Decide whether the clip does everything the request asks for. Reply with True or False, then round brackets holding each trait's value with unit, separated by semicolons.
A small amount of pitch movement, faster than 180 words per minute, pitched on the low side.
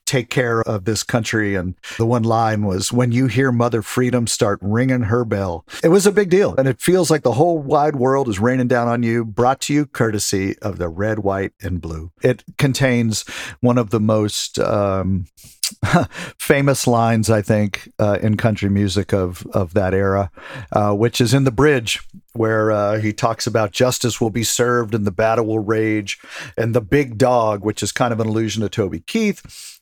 False (3.3 semitones; 200 wpm; 115 Hz)